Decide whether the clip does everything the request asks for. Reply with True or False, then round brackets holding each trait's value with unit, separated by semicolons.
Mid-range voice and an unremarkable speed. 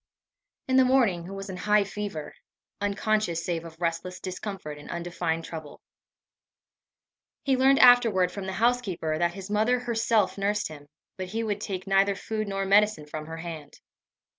False (195 Hz; 165 wpm)